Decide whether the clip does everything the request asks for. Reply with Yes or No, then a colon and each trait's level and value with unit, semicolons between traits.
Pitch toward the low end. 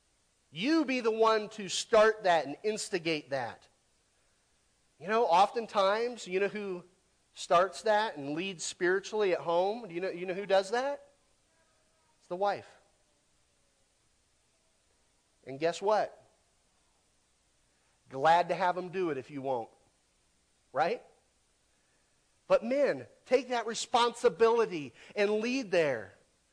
No: high, 195 Hz